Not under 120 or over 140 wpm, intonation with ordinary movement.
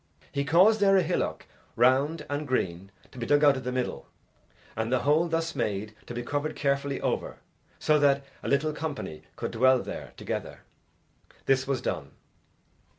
No: average, 170 wpm; average, 3.3 semitones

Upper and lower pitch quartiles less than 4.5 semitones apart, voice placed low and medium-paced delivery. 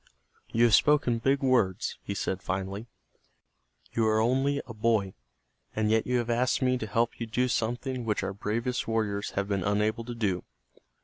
Yes: average, 3.0 semitones; low, 115 Hz; average, 180 wpm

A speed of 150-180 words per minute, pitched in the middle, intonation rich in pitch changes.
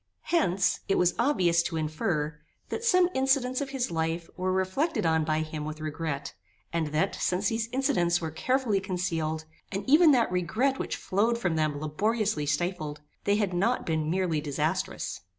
Yes: average, 170 wpm; medium, 180 Hz; wide, 6.6 semitones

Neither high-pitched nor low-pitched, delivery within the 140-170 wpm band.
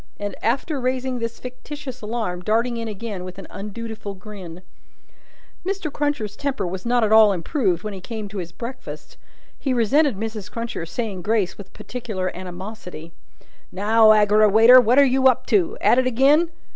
No: high, 220 Hz; average, 165 wpm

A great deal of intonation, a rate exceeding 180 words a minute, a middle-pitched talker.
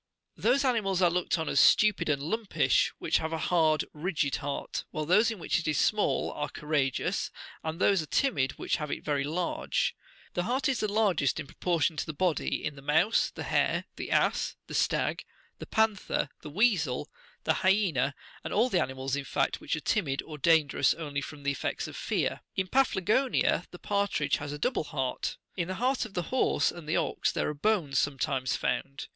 Yes: wide, 5.8 semitones; fast, 205 wpm; medium, 160 Hz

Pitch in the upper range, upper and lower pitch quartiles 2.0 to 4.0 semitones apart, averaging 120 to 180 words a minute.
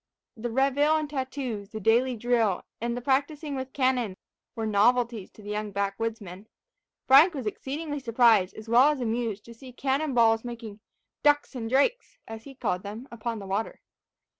Yes: high, 235 Hz; average, 3.6 semitones; average, 175 wpm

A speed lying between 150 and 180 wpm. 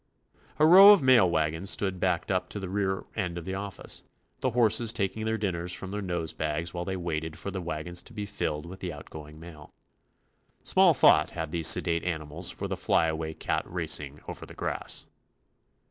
No: average, 200 wpm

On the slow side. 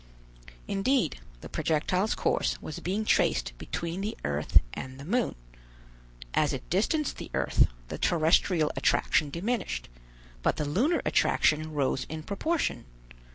Yes: slow, 130 wpm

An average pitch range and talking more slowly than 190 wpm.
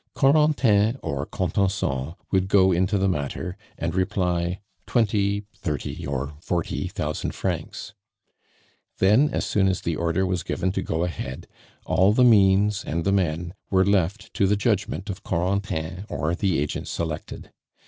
Yes: average, 3.1 semitones; average, 150 wpm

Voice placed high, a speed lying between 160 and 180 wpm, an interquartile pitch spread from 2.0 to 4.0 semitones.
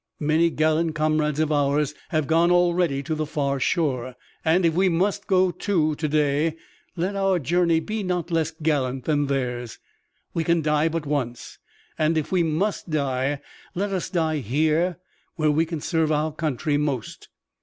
No: medium, 155 Hz; average, 170 wpm; narrow, 2.6 semitones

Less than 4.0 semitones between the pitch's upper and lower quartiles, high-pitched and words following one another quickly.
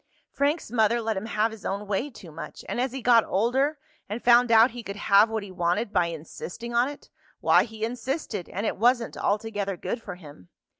Yes: average, 3.3 semitones; high, 225 Hz; fast, 210 wpm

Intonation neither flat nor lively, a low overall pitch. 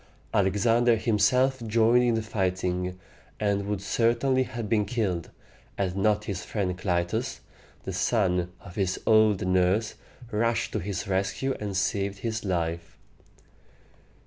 Yes: average, 3.5 semitones; low, 100 Hz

